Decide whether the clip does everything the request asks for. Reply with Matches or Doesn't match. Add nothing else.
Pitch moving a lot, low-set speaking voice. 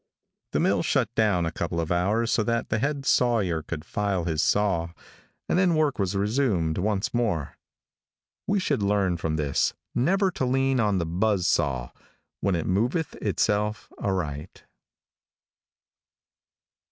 Matches